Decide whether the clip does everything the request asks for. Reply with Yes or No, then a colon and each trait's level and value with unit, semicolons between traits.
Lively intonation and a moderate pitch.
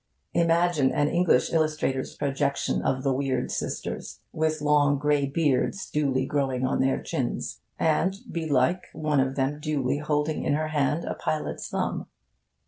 No: narrow, 2.5 semitones; medium, 145 Hz